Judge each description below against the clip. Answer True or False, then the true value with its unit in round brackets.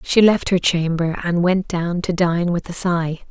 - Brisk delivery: True (220 wpm)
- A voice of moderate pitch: True (175 Hz)